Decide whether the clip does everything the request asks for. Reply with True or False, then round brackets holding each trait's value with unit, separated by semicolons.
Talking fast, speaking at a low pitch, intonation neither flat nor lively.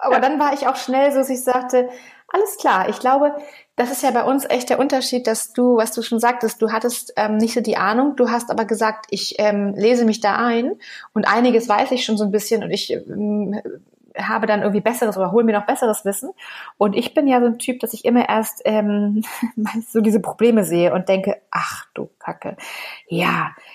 False (220 wpm; 230 Hz; 3.0 semitones)